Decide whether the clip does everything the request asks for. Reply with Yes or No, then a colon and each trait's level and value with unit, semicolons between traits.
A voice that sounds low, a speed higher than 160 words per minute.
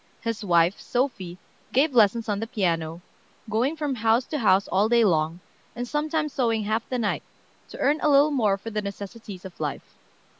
No: high, 220 Hz; average, 185 wpm